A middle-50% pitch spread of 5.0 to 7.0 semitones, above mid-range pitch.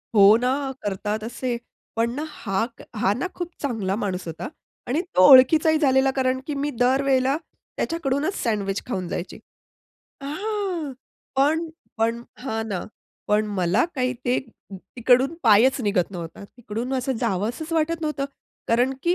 Yes: average, 5.3 semitones; very high, 250 Hz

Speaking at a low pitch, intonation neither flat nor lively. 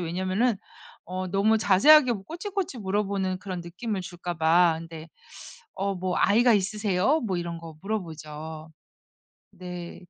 No: medium, 185 Hz; average, 3.7 semitones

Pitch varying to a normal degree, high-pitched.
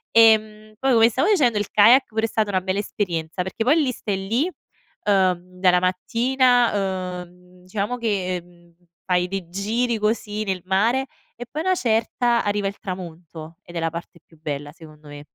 Yes: average, 4.3 semitones; high, 200 Hz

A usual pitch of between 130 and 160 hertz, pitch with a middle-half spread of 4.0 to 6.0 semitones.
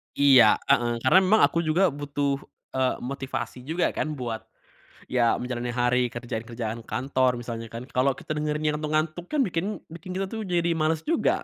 Yes: medium, 140 Hz; average, 4.9 semitones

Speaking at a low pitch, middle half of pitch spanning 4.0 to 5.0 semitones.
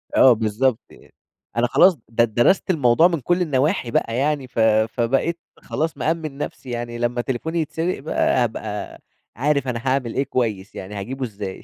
Yes: low, 130 Hz; average, 4.4 semitones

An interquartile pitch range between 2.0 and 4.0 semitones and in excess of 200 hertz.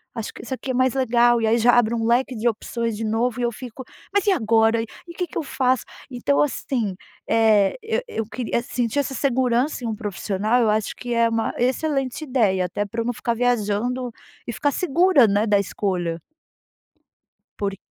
Yes: average, 3.0 semitones; high, 235 Hz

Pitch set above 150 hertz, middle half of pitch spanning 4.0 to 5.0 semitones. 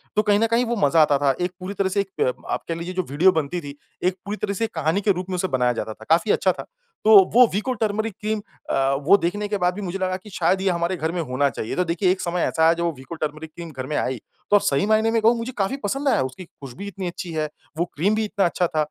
Yes: medium, 185 Hz; average, 4.4 semitones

